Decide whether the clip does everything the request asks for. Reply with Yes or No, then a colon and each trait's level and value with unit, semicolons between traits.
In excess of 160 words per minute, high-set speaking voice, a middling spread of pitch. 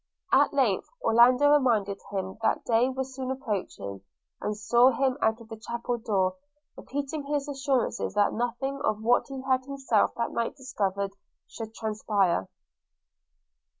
No: average, 145 wpm; high, 235 Hz; average, 3.9 semitones